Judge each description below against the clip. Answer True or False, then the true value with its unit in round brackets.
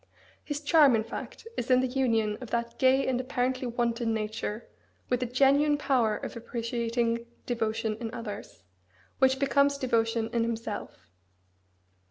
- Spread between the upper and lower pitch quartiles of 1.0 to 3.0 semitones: True (2.5 semitones)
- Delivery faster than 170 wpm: False (145 wpm)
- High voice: True (240 Hz)